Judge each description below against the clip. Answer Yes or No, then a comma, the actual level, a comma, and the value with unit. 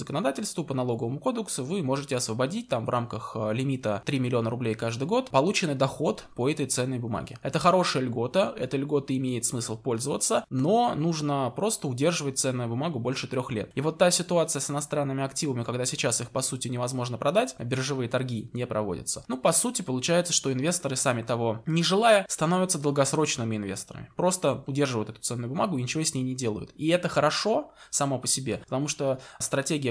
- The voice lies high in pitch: No, low, 135 Hz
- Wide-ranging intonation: No, average, 4.3 semitones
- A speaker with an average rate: No, fast, 180 wpm